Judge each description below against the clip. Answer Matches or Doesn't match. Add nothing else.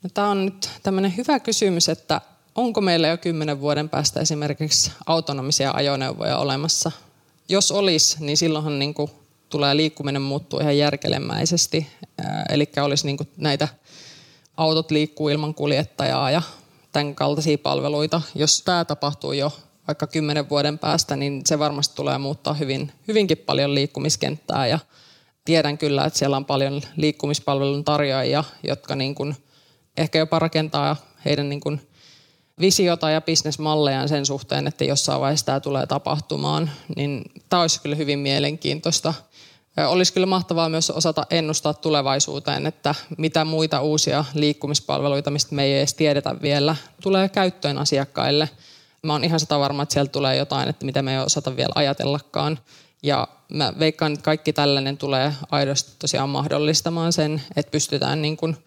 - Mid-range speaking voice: Matches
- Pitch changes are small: Matches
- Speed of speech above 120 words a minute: Matches